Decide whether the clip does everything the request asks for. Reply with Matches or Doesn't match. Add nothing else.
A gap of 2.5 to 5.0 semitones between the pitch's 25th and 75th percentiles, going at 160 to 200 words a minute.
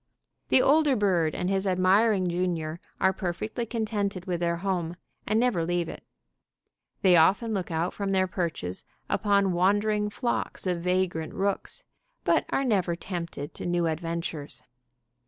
Doesn't match